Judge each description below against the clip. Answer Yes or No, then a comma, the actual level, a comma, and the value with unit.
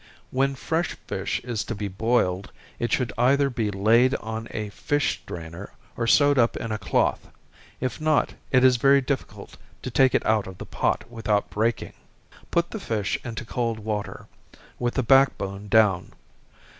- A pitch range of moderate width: Yes, average, 3.8 semitones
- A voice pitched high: No, low, 115 Hz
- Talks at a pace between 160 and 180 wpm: Yes, average, 170 wpm